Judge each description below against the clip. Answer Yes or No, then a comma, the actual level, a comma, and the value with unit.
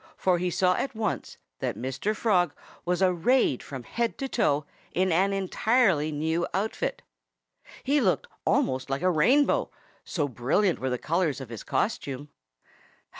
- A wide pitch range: Yes, wide, 6.4 semitones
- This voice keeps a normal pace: Yes, average, 150 wpm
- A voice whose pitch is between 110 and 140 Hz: No, medium, 180 Hz